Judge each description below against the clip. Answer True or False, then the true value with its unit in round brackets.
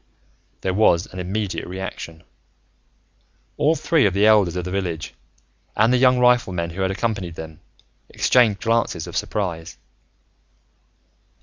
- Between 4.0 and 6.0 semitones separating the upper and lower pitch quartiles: True (4.6 semitones)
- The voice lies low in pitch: True (95 Hz)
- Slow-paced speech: True (130 wpm)